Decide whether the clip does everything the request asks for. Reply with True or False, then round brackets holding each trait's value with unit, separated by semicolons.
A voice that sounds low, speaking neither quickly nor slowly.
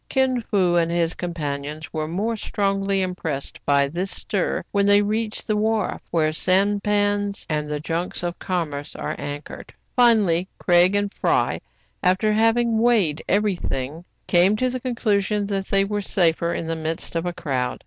False (185 Hz; 170 wpm)